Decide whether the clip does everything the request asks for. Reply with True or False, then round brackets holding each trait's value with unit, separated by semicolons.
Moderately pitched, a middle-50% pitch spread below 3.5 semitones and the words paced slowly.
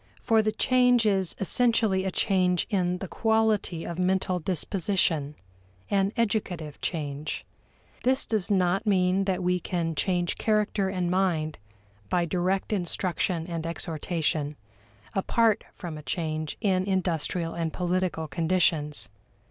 True (180 Hz; 2.9 semitones; 125 wpm)